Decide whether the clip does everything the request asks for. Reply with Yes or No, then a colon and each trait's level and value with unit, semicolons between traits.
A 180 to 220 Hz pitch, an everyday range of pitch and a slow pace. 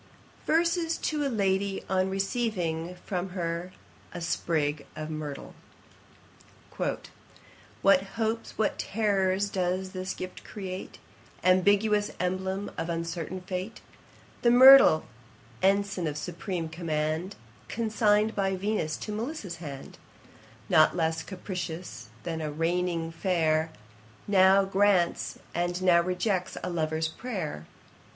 Yes: medium, 185 Hz; average, 3.3 semitones; slow, 115 wpm